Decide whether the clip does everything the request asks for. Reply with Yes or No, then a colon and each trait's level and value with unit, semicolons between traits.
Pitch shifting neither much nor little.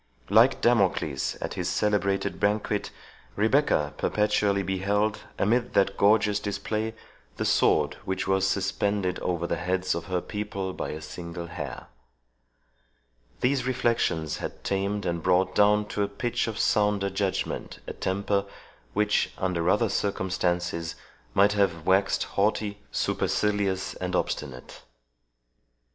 No: narrow, 2.2 semitones